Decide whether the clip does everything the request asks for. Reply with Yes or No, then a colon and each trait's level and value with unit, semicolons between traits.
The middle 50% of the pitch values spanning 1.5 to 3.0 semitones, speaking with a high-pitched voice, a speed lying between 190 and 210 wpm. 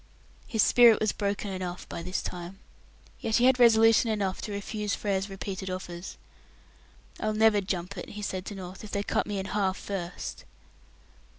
No: narrow, 2.4 semitones; high, 200 Hz; average, 175 wpm